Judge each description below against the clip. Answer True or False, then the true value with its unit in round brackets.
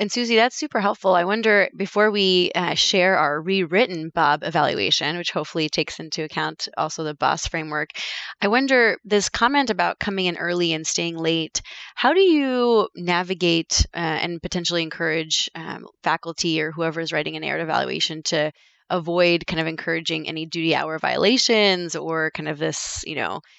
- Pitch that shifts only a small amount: False (4.0 semitones)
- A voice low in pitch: False (170 Hz)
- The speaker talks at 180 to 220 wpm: False (170 wpm)